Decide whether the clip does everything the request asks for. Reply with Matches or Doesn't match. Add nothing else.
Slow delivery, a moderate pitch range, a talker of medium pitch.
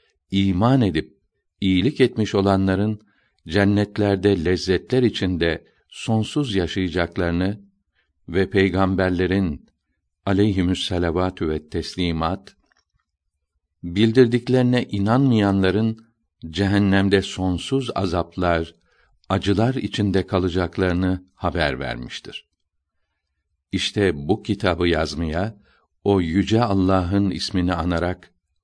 Doesn't match